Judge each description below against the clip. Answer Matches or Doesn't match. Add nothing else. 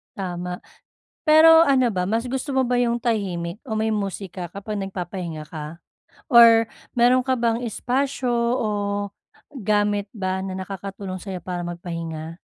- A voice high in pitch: Matches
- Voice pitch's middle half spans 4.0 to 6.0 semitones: Matches